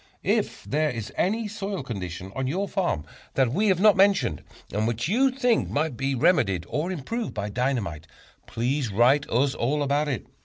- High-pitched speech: No, medium, 140 Hz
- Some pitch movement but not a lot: No, wide, 8.4 semitones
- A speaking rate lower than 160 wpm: No, average, 180 wpm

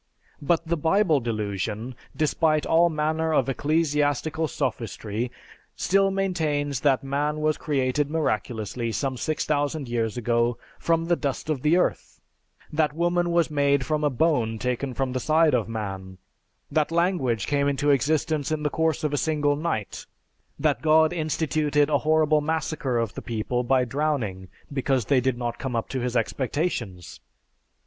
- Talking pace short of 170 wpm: Yes, average, 155 wpm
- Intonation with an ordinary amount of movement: Yes, average, 4.2 semitones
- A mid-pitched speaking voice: Yes, medium, 145 Hz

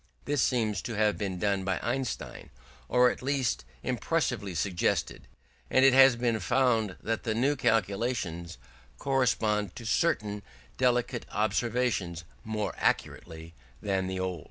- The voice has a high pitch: No, low, 110 Hz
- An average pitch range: Yes, average, 4.4 semitones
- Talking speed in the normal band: No, slow, 130 wpm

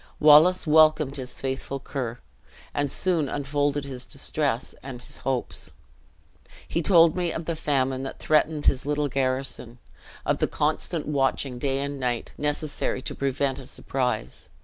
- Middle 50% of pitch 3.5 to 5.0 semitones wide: No, narrow, 2.4 semitones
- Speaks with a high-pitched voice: No, medium, 140 Hz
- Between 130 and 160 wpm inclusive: Yes, average, 150 wpm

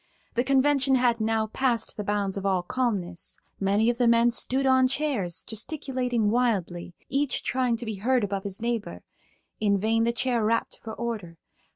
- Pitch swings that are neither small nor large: Yes, average, 3.7 semitones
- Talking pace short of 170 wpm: No, average, 175 wpm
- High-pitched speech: Yes, high, 230 Hz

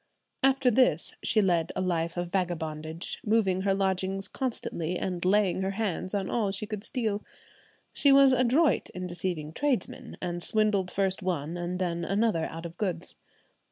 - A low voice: No, high, 190 Hz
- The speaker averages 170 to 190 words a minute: No, average, 160 wpm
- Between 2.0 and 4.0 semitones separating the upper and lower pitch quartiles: Yes, average, 3.6 semitones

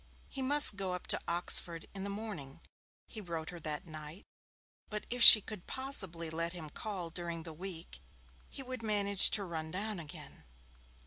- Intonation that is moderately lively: Yes, average, 4.2 semitones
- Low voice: No, medium, 180 Hz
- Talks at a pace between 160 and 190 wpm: Yes, average, 175 wpm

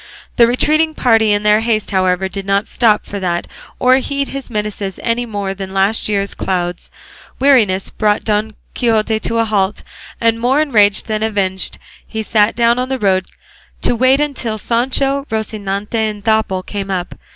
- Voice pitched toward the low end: No, high, 215 Hz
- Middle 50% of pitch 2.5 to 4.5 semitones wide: Yes, average, 3.2 semitones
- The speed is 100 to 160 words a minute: No, average, 175 wpm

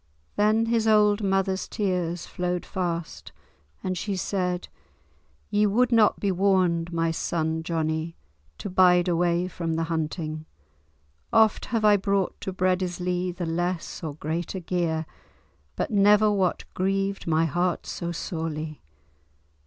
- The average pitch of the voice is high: No, medium, 180 Hz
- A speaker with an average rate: No, slow, 130 wpm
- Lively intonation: No, average, 3.0 semitones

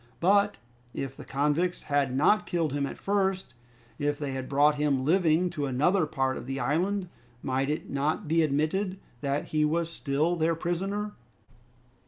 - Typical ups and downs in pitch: Yes, average, 4.2 semitones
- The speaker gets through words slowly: No, average, 165 wpm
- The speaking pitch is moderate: Yes, medium, 155 Hz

